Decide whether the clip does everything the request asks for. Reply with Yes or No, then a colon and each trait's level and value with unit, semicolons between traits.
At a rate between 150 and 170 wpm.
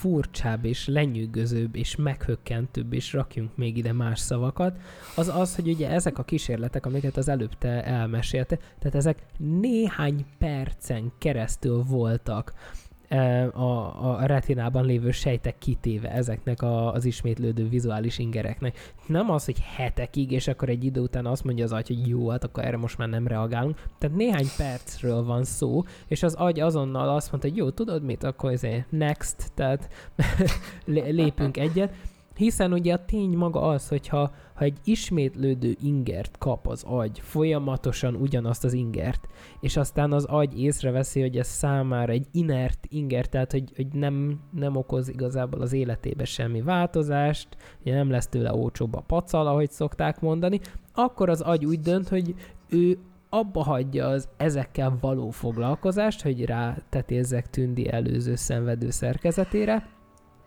Yes: fast, 155 wpm